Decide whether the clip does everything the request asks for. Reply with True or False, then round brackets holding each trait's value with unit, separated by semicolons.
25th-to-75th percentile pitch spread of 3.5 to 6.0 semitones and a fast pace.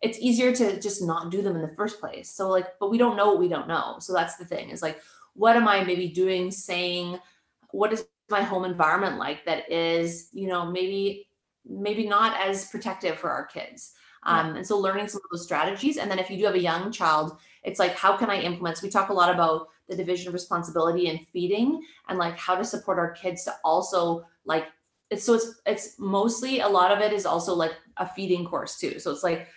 False (2.9 semitones; 235 wpm)